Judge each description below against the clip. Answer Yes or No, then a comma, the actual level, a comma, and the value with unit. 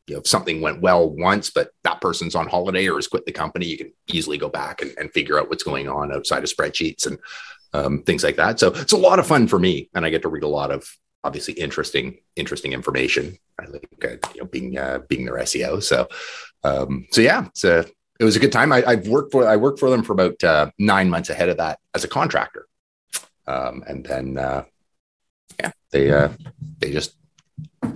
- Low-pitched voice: Yes, low, 125 Hz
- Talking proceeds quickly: Yes, fast, 220 wpm